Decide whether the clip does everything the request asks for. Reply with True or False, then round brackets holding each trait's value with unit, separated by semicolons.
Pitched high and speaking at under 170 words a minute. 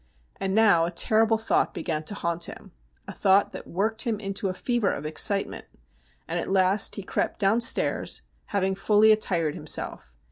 False (195 Hz; 185 wpm)